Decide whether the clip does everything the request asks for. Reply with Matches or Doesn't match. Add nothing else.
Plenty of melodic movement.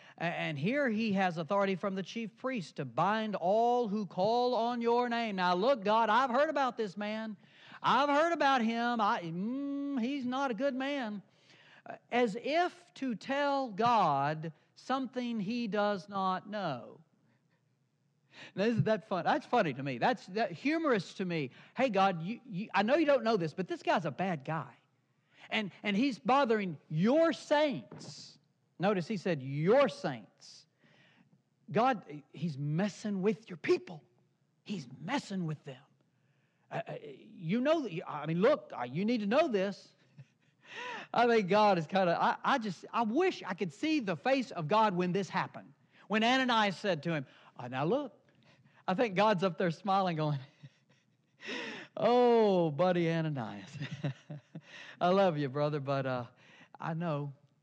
Matches